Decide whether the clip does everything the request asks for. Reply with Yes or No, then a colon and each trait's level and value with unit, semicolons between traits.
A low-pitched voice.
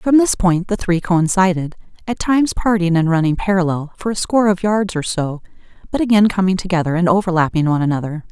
No: medium, 185 Hz